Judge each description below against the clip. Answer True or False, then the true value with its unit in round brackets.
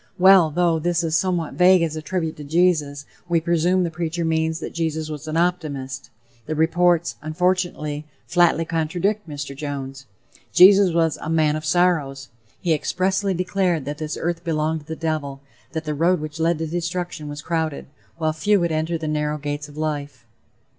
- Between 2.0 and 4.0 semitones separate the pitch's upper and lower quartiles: True (2.5 semitones)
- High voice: False (160 Hz)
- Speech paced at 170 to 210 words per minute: True (180 wpm)